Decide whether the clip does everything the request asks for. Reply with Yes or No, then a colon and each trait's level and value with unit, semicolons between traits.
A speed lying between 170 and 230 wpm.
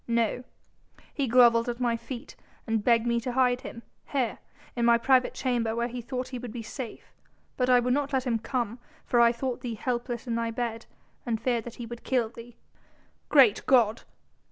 Yes: average, 200 wpm